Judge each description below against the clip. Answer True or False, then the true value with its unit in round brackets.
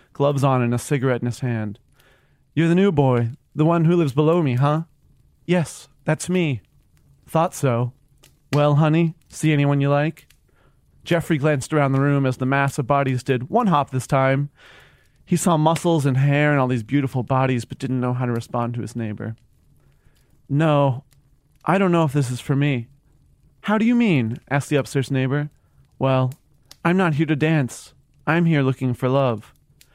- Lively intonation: False (3.3 semitones)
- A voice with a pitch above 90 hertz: True (140 Hz)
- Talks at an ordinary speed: True (185 wpm)